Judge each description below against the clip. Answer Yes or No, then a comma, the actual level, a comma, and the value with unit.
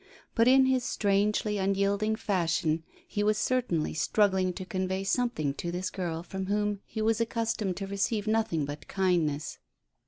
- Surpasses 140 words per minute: Yes, average, 155 wpm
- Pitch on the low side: No, high, 195 Hz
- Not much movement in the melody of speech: No, average, 3.3 semitones